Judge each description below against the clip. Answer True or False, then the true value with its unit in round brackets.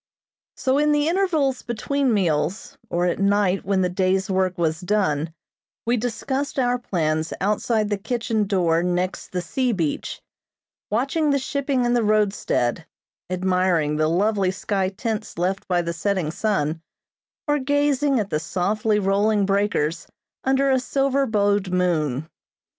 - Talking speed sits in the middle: True (145 wpm)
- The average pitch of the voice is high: True (200 Hz)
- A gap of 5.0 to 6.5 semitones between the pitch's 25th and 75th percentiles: True (5.5 semitones)